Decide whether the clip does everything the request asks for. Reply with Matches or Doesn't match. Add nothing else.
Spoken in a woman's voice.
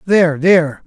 Doesn't match